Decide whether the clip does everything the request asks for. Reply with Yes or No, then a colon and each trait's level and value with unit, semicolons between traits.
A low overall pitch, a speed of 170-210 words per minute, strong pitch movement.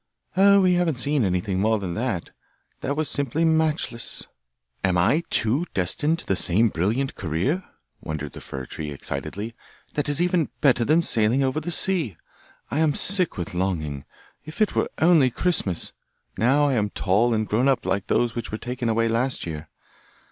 Yes: low, 120 Hz; average, 175 wpm; wide, 8.0 semitones